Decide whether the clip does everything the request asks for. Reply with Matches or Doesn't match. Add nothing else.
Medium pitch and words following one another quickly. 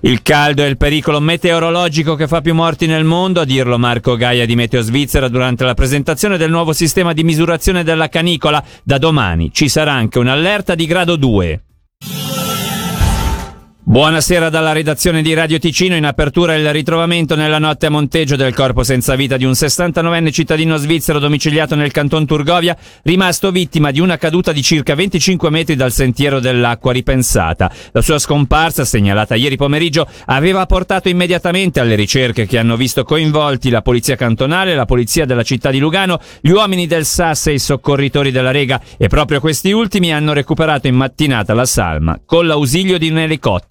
Matches